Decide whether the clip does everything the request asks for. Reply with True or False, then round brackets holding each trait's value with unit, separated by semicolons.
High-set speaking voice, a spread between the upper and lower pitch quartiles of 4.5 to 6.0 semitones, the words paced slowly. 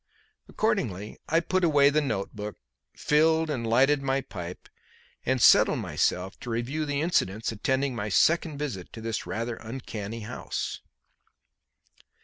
False (130 Hz; 5.5 semitones; 130 wpm)